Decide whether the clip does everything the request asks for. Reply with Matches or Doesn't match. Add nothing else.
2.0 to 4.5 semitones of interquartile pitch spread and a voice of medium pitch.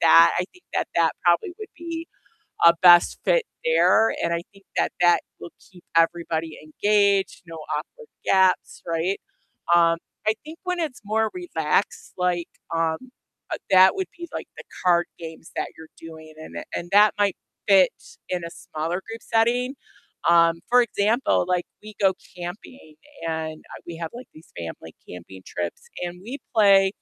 Doesn't match